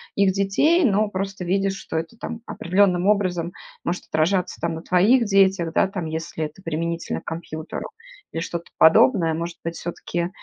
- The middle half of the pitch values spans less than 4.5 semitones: Yes, average, 2.9 semitones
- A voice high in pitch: No, medium, 180 Hz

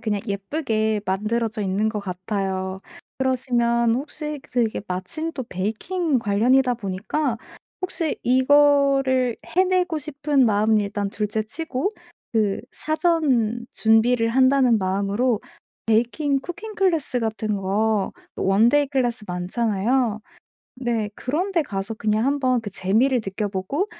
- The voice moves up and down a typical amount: Yes, average, 4.8 semitones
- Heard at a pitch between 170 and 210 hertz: No, high, 235 Hz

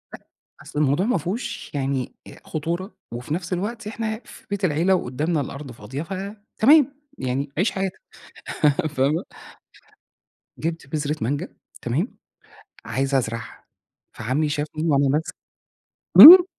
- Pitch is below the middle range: No, medium, 155 Hz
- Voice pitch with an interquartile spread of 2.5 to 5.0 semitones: No, wide, 5.6 semitones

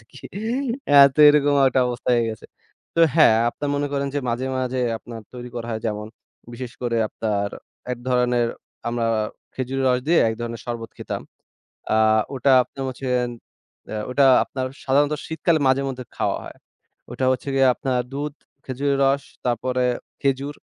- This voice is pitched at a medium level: No, low, 130 Hz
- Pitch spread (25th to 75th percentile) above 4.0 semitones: No, narrow, 2.6 semitones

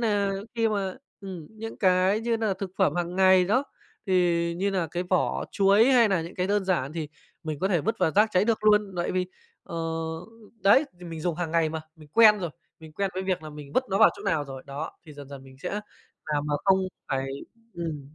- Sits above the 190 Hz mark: No, medium, 185 Hz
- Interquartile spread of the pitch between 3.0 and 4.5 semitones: Yes, average, 4.1 semitones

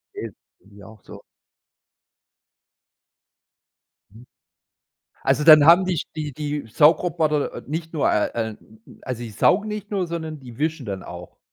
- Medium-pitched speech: Yes, medium, 150 Hz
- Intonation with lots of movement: Yes, wide, 6.2 semitones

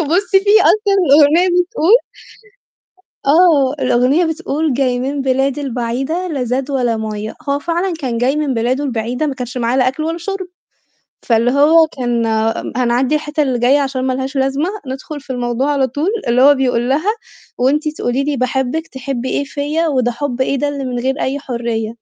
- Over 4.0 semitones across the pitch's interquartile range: No, average, 3.3 semitones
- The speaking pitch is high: Yes, very high, 270 Hz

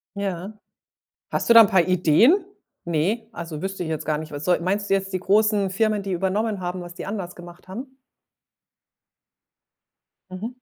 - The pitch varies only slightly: No, average, 3.1 semitones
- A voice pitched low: No, high, 190 Hz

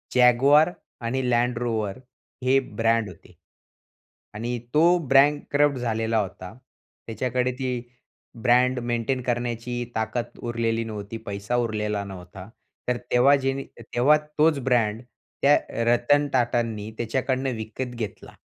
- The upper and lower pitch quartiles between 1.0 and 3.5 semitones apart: Yes, average, 2.7 semitones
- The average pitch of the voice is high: No, low, 120 Hz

